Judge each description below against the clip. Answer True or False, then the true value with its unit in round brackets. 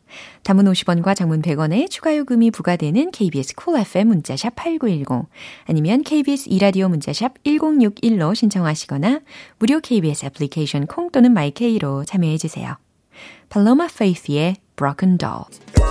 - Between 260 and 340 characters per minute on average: False (360 characters per minute)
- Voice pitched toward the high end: True (195 Hz)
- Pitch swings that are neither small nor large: False (8.0 semitones)